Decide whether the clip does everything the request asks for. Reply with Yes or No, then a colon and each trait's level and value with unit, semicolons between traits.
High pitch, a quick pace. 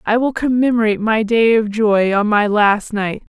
No: high, 220 Hz; average, 195 wpm